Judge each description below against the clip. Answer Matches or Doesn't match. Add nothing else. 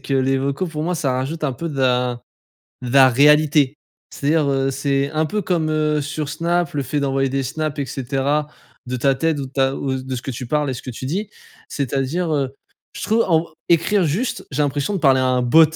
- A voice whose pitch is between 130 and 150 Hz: Matches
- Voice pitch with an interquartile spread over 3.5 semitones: Doesn't match